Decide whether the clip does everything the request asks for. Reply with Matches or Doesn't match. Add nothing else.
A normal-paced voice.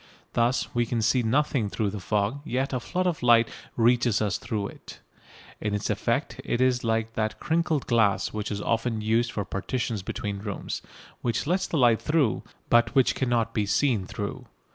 Matches